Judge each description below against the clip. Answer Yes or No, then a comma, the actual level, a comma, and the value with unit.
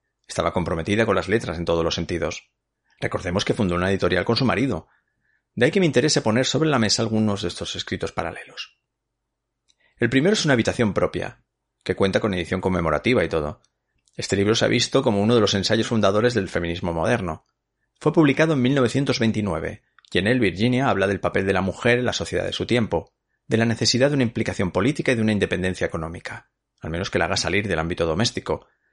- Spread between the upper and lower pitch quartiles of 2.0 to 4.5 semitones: No, average, 5.0 semitones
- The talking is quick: Yes, fast, 205 wpm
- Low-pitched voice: Yes, low, 105 Hz